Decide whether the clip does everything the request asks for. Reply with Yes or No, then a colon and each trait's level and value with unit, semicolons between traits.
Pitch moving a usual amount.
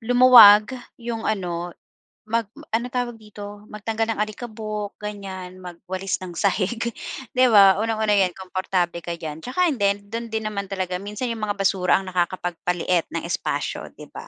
Yes: average, 3.2 semitones